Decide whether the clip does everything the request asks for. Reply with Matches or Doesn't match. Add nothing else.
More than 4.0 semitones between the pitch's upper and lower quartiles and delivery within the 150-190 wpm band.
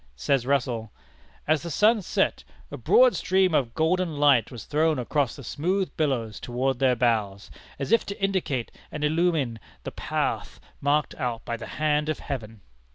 Matches